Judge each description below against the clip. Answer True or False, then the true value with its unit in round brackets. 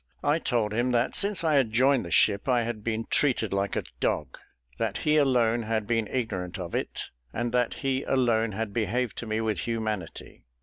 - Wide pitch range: False (2.9 semitones)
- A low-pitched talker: True (115 Hz)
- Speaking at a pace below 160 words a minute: False (200 wpm)